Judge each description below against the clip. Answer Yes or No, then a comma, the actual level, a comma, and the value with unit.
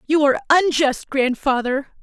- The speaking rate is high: No, slow, 120 wpm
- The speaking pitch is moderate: No, very high, 285 Hz